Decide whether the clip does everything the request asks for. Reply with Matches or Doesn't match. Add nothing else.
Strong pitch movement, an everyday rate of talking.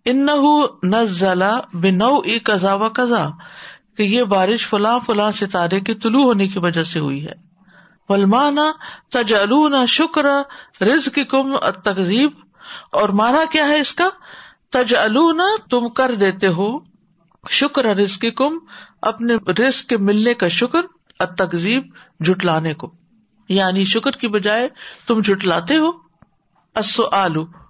Matches